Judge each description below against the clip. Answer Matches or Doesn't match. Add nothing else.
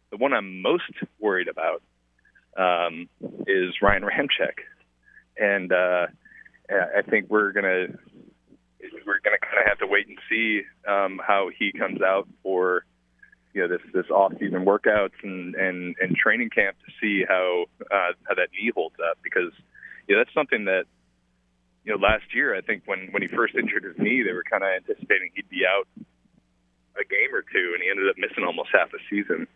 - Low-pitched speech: Matches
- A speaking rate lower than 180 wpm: Doesn't match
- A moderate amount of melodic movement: Doesn't match